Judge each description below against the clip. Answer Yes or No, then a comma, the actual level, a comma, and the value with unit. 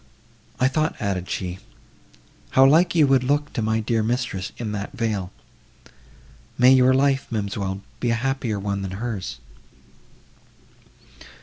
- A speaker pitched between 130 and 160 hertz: No, low, 115 Hz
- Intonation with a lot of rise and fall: No, average, 4.8 semitones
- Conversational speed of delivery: No, slow, 130 wpm